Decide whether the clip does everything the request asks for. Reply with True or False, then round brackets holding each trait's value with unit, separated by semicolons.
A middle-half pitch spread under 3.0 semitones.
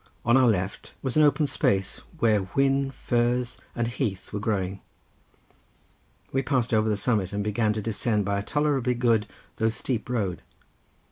False (3.7 semitones)